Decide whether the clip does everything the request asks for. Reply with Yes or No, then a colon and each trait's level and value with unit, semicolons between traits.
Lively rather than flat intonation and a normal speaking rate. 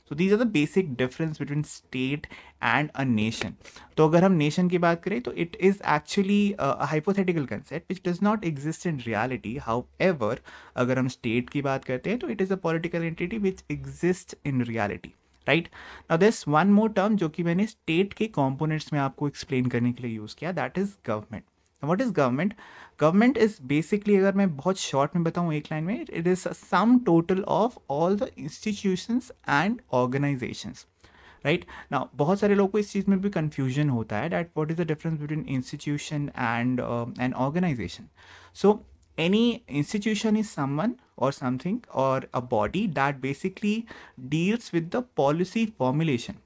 Yes: wide, 6.4 semitones; average, 165 wpm